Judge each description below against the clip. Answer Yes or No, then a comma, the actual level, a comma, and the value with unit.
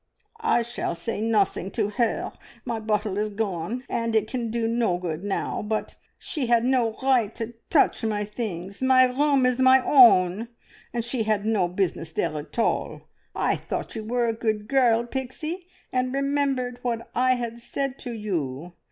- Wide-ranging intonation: No, average, 3.3 semitones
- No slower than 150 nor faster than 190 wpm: Yes, average, 175 wpm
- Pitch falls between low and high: No, high, 230 Hz